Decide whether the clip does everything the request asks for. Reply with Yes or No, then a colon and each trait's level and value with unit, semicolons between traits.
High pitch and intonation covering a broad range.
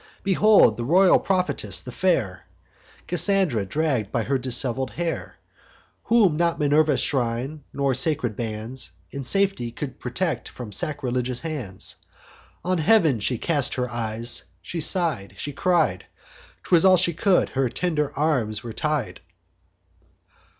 No: medium, 140 Hz; wide, 6.1 semitones